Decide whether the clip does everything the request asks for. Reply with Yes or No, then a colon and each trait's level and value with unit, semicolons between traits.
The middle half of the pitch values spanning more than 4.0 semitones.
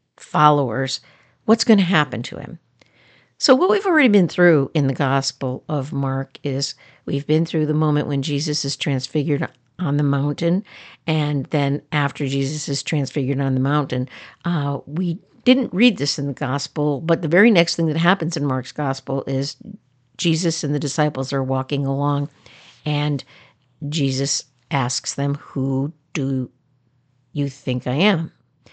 No: narrow, 2.6 semitones